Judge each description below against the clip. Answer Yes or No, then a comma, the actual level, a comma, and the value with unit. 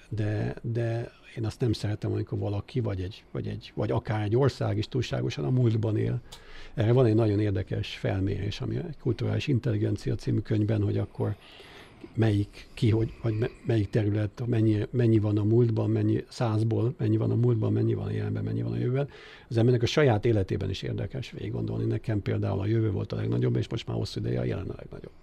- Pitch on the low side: Yes, low, 110 Hz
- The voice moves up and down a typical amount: No, narrow, 2.1 semitones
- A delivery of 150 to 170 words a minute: No, average, 200 wpm